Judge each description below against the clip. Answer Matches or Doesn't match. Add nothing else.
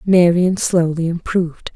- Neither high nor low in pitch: Matches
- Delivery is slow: Matches